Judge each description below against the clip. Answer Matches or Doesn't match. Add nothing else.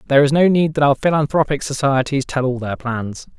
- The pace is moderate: Doesn't match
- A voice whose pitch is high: Doesn't match